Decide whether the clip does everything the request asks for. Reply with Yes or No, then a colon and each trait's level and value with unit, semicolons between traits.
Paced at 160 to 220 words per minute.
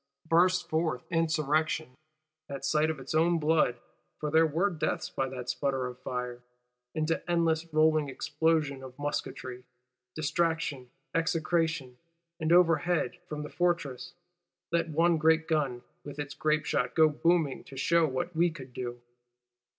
No: average, 140 wpm